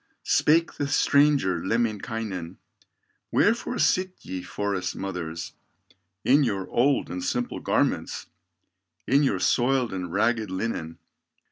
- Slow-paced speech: Yes, slow, 110 wpm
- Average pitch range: No, wide, 6.4 semitones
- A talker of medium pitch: No, low, 110 Hz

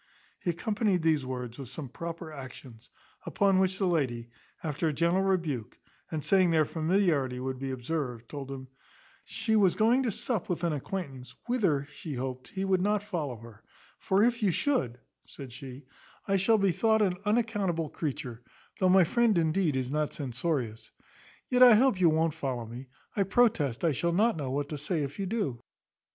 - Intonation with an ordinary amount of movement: No, wide, 6.5 semitones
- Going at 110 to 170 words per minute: No, average, 185 wpm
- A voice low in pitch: No, medium, 160 Hz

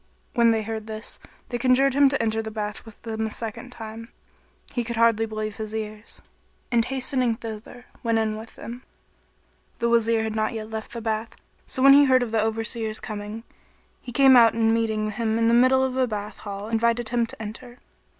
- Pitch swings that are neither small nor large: No, narrow, 1.7 semitones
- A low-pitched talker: No, high, 225 Hz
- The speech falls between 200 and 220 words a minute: Yes, fast, 205 wpm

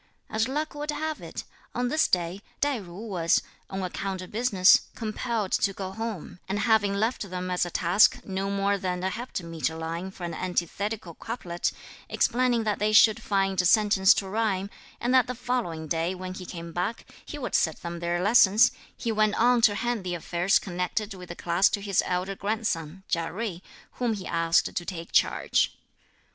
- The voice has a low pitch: No, high, 195 Hz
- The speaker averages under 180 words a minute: No, average, 190 wpm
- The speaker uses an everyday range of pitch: Yes, average, 3.8 semitones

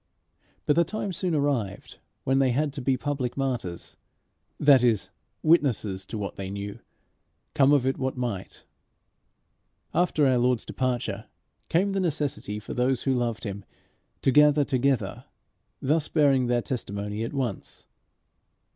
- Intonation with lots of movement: No, average, 4.2 semitones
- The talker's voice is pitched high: No, low, 130 Hz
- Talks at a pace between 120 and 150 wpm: Yes, average, 145 wpm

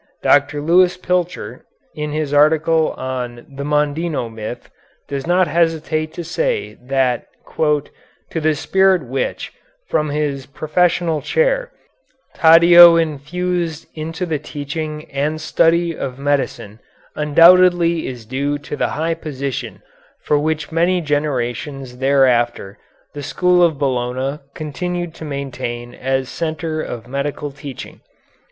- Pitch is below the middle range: No, medium, 150 Hz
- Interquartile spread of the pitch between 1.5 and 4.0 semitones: Yes, average, 3.5 semitones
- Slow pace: Yes, slow, 120 wpm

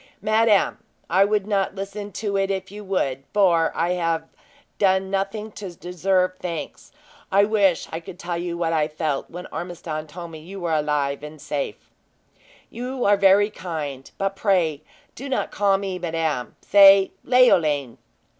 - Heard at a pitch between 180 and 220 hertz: Yes, medium, 185 Hz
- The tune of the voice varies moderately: Yes, average, 3.5 semitones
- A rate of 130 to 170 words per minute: Yes, average, 160 wpm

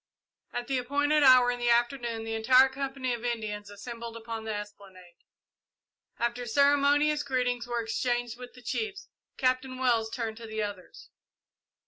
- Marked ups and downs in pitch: No, average, 2.7 semitones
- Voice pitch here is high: Yes, high, 240 Hz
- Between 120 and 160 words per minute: Yes, average, 150 wpm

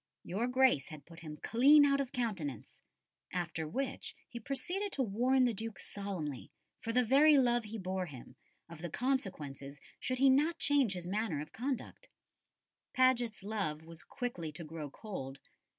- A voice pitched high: Yes, high, 220 Hz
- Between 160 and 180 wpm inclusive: Yes, average, 165 wpm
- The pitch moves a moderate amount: No, wide, 7.8 semitones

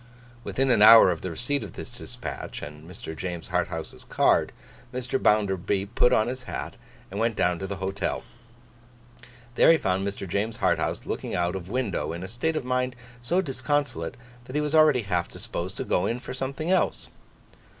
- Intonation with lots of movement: Yes, wide, 5.7 semitones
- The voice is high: No, low, 110 Hz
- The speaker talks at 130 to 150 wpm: No, average, 185 wpm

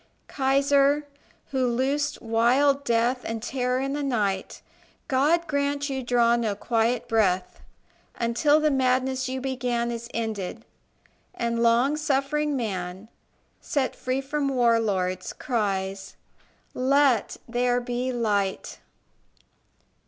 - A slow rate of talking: Yes, slow, 115 wpm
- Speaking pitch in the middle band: No, very high, 250 Hz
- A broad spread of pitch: No, average, 3.2 semitones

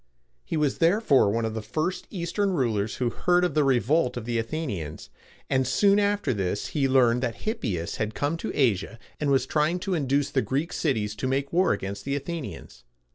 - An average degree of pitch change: No, wide, 6.3 semitones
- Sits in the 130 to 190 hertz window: Yes, low, 135 Hz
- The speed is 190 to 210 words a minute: Yes, average, 195 wpm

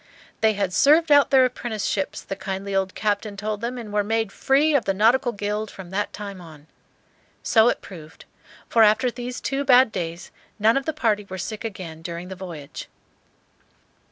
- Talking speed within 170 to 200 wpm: Yes, average, 185 wpm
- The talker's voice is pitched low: No, high, 210 Hz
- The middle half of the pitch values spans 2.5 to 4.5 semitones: Yes, average, 4.1 semitones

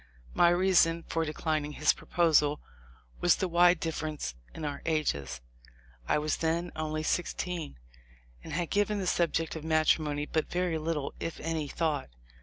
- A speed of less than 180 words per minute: Yes, average, 150 wpm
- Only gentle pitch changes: Yes, narrow, 2.1 semitones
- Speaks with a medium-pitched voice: Yes, medium, 160 Hz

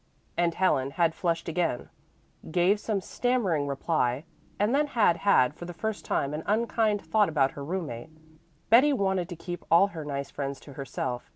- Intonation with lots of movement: Yes, wide, 6.3 semitones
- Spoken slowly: No, average, 175 wpm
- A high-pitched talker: No, medium, 170 Hz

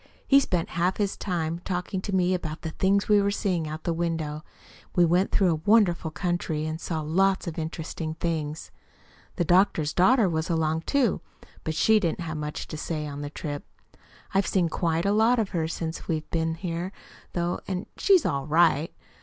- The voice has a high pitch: No, medium, 170 Hz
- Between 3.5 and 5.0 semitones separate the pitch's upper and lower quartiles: No, average, 3.1 semitones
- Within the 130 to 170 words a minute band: No, average, 190 wpm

